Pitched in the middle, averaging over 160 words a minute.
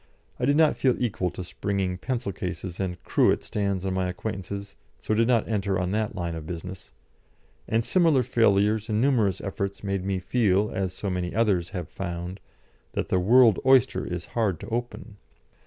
No: low, 100 Hz; average, 180 wpm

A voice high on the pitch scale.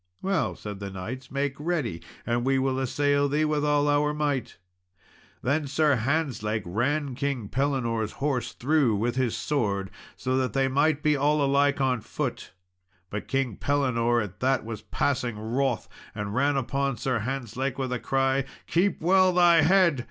No: low, 135 Hz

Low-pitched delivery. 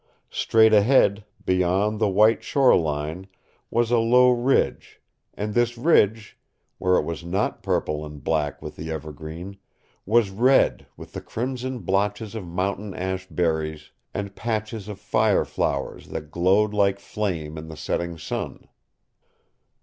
Yes: low, 100 Hz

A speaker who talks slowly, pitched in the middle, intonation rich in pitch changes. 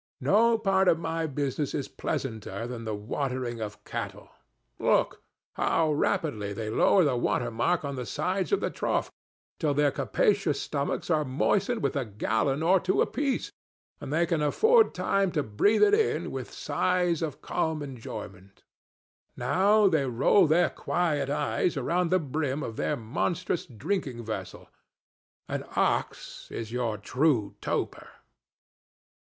No: average, 145 wpm; medium, 150 Hz; wide, 6.6 semitones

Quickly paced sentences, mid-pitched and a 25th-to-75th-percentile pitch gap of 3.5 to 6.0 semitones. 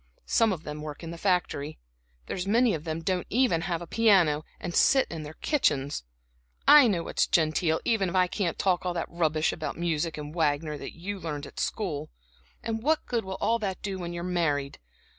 Yes: fast, 210 wpm; medium, 175 Hz; average, 4.1 semitones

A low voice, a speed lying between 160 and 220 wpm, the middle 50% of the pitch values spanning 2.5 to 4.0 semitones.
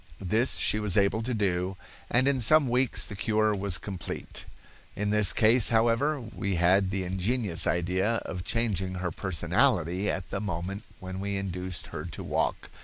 Yes: low, 100 Hz; average, 170 wpm; average, 3.3 semitones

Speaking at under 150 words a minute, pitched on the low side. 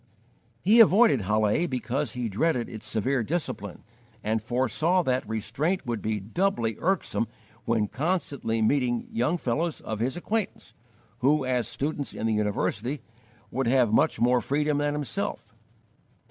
Yes: average, 140 wpm; low, 125 Hz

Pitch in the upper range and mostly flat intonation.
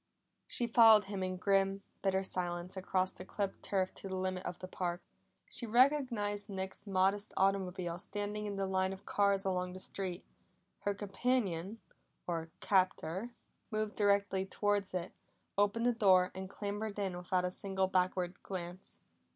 Yes: high, 195 Hz; narrow, 1.8 semitones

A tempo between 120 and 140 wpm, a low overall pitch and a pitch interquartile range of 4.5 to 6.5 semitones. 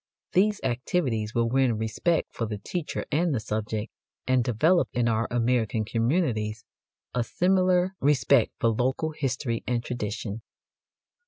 Yes: slow, 135 wpm; low, 120 Hz; average, 5.2 semitones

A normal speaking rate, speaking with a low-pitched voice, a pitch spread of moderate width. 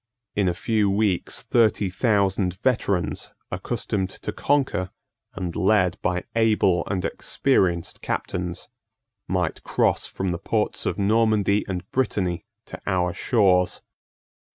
No: slow, 120 wpm; very low, 95 Hz; average, 3.0 semitones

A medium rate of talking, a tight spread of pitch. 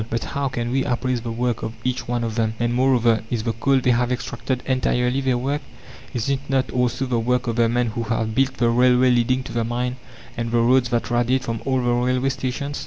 No: fast, 240 wpm; narrow, 1.5 semitones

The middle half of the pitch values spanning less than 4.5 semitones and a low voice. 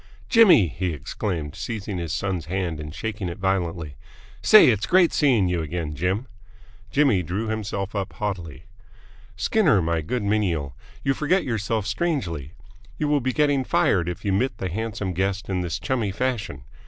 No: average, 4.9 semitones; low, 100 Hz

